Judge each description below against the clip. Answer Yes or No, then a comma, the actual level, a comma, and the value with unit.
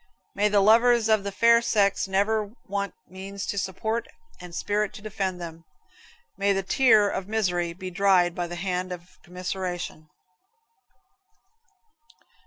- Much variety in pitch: No, average, 2.7 semitones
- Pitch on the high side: Yes, high, 195 Hz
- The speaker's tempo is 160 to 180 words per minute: No, average, 140 wpm